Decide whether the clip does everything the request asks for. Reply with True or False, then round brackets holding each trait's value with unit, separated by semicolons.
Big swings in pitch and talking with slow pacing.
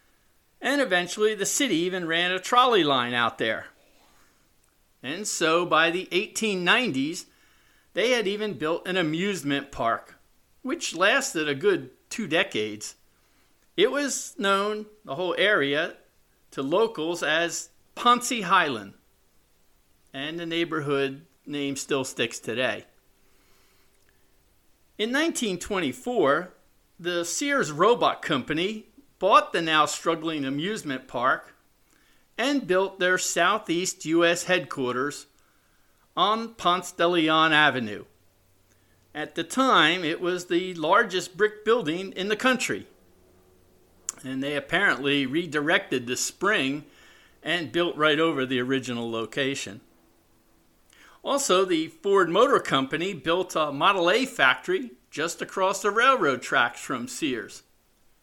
True (7.4 semitones; 115 wpm)